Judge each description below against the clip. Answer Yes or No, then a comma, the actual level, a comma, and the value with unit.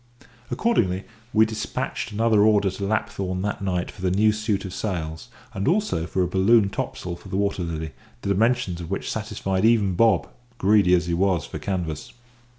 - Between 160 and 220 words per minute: Yes, average, 180 wpm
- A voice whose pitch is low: Yes, very low, 95 Hz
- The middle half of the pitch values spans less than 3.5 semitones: Yes, average, 3.0 semitones